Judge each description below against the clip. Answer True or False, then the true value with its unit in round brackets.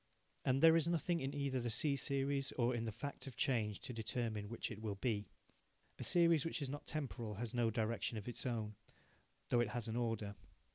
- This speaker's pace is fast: True (210 wpm)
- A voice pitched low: True (120 Hz)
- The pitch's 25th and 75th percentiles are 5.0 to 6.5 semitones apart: False (3.9 semitones)